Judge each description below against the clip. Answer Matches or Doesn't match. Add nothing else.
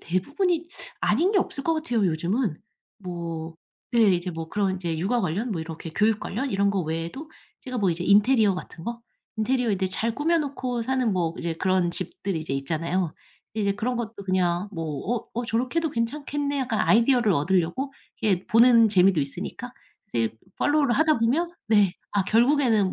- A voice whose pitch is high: Matches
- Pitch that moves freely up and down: Matches